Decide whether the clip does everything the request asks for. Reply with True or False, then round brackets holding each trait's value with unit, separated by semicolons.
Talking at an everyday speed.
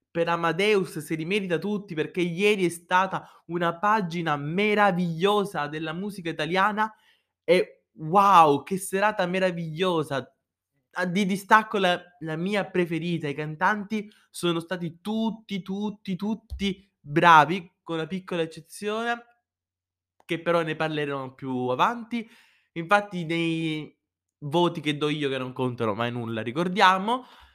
True (125 wpm)